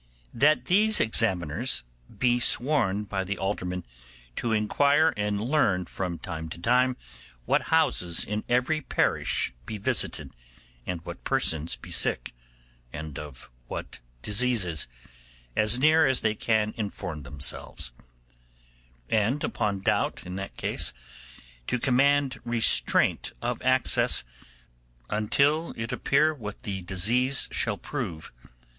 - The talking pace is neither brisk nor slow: No, slow, 120 wpm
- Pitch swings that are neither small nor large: No, wide, 6.0 semitones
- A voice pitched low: Yes, low, 110 Hz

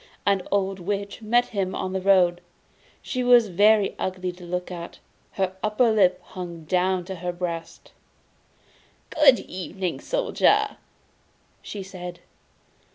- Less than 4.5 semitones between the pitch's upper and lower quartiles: Yes, narrow, 2.5 semitones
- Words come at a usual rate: No, slow, 130 wpm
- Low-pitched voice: No, high, 190 Hz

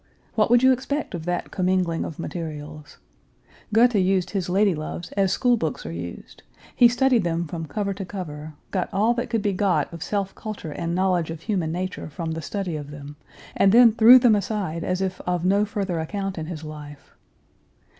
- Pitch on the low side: No, medium, 185 Hz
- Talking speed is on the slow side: No, average, 195 wpm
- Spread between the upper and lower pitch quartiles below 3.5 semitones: No, average, 4.1 semitones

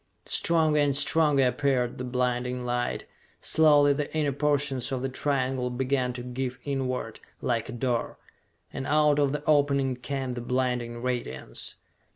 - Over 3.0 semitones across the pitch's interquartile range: No, narrow, 2.5 semitones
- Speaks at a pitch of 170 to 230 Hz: No, low, 130 Hz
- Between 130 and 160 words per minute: Yes, average, 150 wpm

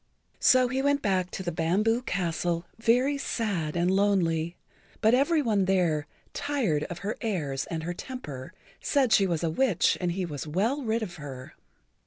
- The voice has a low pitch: No, high, 190 Hz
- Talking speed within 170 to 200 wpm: Yes, average, 175 wpm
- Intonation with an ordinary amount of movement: No, wide, 6.0 semitones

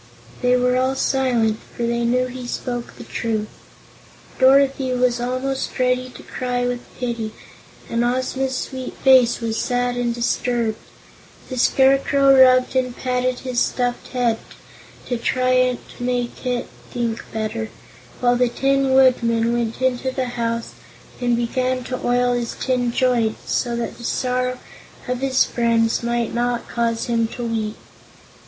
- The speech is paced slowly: No, average, 145 wpm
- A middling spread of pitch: No, narrow, 1.3 semitones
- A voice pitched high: Yes, high, 245 Hz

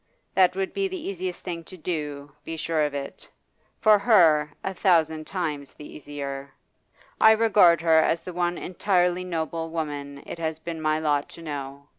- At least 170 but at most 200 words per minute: Yes, average, 175 wpm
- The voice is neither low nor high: Yes, medium, 165 Hz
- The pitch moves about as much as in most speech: Yes, average, 3.4 semitones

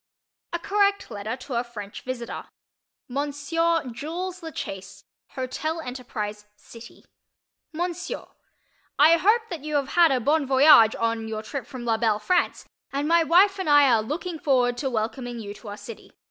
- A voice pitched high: Yes, very high, 270 Hz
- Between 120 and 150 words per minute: No, average, 165 wpm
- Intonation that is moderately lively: No, wide, 6.3 semitones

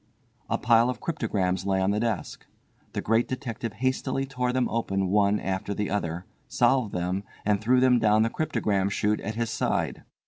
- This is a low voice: Yes, low, 110 Hz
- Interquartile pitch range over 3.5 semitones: Yes, average, 3.9 semitones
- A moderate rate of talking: Yes, average, 180 wpm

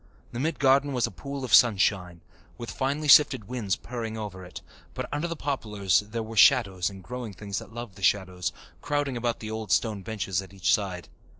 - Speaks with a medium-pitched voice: No, low, 110 Hz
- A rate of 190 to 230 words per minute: Yes, average, 200 wpm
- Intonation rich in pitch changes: No, average, 4.8 semitones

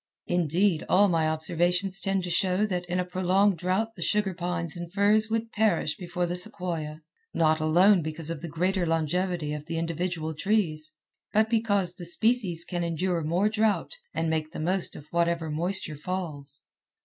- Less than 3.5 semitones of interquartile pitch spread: Yes, average, 3.0 semitones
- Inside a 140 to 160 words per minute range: No, average, 170 wpm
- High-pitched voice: No, medium, 175 Hz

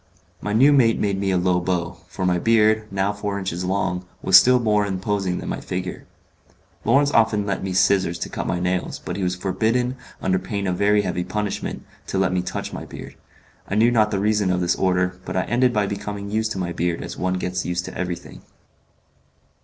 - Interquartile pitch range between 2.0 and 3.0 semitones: Yes, narrow, 2.6 semitones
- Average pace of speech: No, fast, 215 wpm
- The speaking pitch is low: Yes, very low, 95 Hz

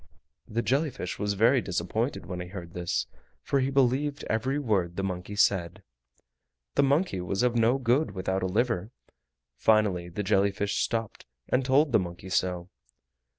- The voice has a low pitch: Yes, low, 105 Hz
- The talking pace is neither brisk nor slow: Yes, average, 165 wpm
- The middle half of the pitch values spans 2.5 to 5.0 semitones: No, wide, 5.6 semitones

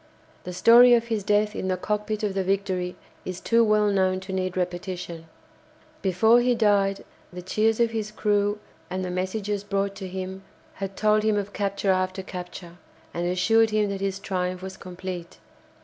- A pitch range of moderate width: No, narrow, 2.3 semitones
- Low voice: No, high, 195 Hz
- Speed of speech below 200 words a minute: Yes, average, 180 wpm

